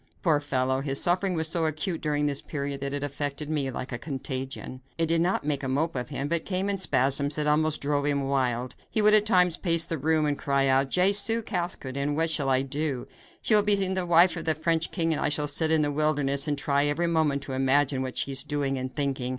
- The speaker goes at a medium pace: No, fast, 240 wpm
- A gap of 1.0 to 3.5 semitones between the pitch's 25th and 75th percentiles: Yes, average, 3.2 semitones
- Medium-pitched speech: Yes, medium, 145 Hz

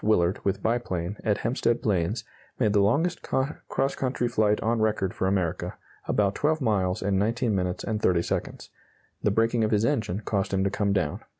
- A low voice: Yes, low, 105 Hz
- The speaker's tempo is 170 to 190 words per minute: Yes, average, 185 wpm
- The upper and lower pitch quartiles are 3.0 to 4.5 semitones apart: Yes, average, 3.4 semitones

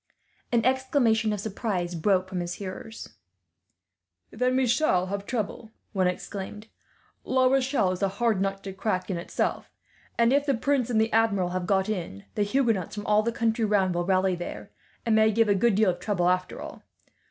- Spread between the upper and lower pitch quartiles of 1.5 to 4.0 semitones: Yes, average, 3.7 semitones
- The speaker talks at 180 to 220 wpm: Yes, average, 190 wpm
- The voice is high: Yes, high, 210 Hz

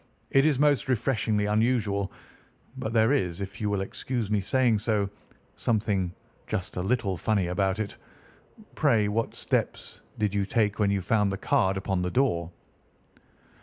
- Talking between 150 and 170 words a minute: Yes, average, 160 wpm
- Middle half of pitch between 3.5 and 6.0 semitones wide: No, average, 3.1 semitones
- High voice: No, low, 105 Hz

